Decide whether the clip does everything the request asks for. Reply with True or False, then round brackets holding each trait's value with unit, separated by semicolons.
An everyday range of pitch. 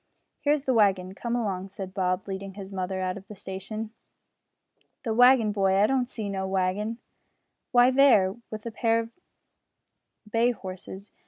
True (3.2 semitones)